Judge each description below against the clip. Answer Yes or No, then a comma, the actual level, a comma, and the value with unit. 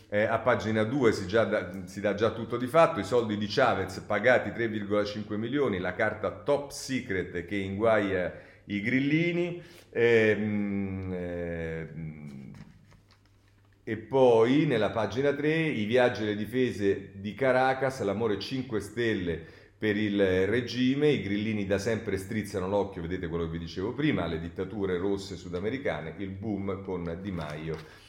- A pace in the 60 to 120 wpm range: No, average, 145 wpm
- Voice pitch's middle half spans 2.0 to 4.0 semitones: Yes, average, 3.5 semitones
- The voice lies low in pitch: Yes, low, 105 Hz